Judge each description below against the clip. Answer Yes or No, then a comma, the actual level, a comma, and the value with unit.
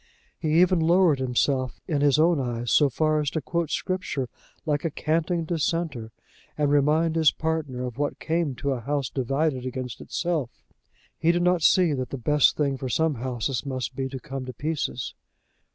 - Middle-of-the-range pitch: Yes, medium, 145 Hz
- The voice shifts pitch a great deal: No, average, 3.8 semitones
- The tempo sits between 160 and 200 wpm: Yes, average, 185 wpm